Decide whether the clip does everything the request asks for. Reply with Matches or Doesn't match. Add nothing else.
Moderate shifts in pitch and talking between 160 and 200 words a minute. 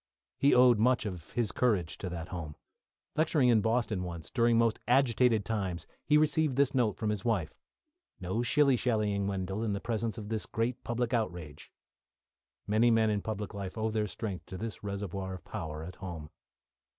Matches